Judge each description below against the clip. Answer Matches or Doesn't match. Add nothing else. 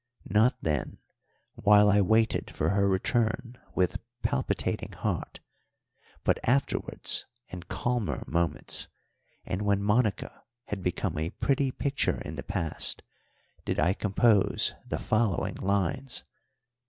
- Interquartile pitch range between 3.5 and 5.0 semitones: Matches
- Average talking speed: Doesn't match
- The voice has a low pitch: Matches